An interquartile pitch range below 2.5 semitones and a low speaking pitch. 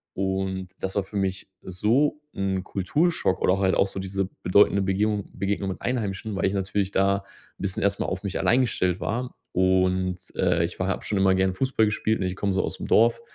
Yes: narrow, 1.7 semitones; very low, 95 Hz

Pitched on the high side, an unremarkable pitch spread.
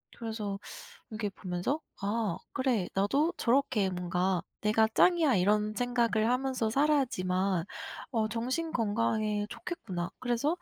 Yes: high, 220 Hz; average, 4.4 semitones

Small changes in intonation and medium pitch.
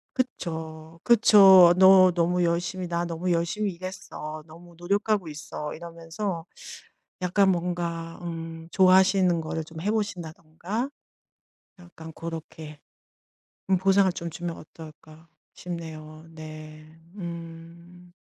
Yes: narrow, 2.3 semitones; medium, 170 Hz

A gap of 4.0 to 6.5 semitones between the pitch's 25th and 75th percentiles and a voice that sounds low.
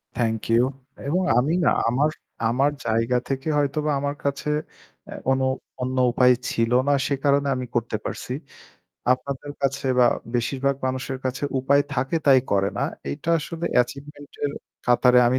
No: narrow, 2.4 semitones; low, 130 Hz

